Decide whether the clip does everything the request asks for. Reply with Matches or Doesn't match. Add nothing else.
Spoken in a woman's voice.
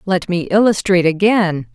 Matches